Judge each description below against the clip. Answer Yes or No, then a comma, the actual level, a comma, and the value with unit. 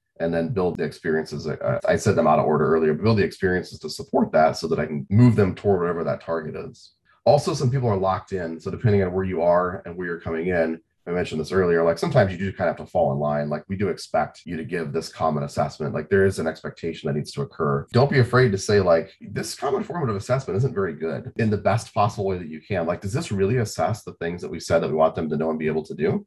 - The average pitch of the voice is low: Yes, very low, 95 Hz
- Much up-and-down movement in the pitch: Yes, wide, 6.4 semitones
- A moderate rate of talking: No, fast, 280 wpm